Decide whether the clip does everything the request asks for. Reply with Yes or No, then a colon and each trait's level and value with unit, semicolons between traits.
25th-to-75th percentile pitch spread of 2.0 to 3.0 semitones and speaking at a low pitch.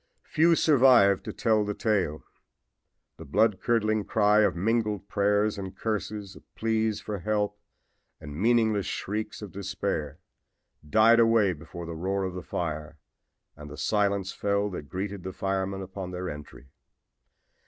Yes: average, 2.7 semitones; low, 100 Hz